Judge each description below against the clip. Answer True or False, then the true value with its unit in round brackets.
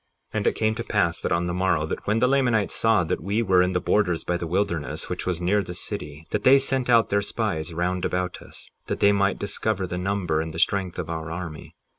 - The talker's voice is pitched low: True (90 Hz)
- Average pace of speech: False (250 wpm)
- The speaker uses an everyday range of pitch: True (3.7 semitones)